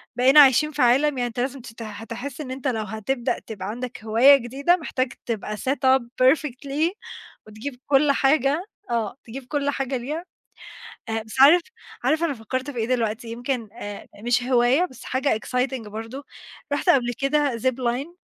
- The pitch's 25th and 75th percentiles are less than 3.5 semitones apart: Yes, average, 3.1 semitones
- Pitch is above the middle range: Yes, very high, 255 Hz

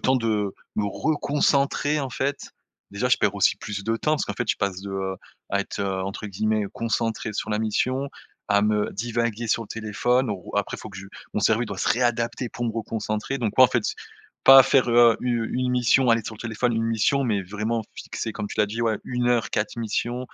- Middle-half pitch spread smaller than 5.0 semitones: Yes, average, 2.8 semitones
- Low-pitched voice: Yes, low, 115 Hz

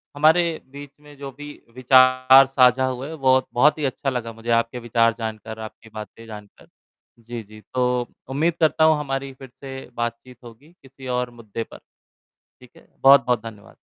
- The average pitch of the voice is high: No, low, 130 Hz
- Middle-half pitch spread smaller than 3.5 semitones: Yes, average, 2.8 semitones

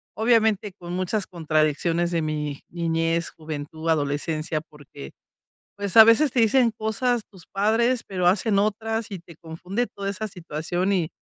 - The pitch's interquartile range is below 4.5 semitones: No, average, 5.2 semitones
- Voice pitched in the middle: Yes, medium, 180 Hz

